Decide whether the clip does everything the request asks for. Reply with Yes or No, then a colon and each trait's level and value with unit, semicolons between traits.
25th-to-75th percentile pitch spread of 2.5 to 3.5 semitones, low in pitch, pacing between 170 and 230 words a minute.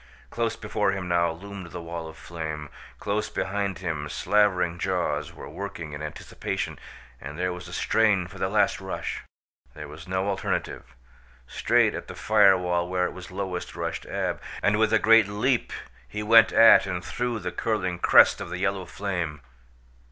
Yes: average, 3.2 semitones; very low, 90 Hz; average, 175 wpm